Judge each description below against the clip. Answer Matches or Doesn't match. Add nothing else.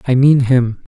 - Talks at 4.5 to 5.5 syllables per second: Doesn't match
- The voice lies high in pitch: Doesn't match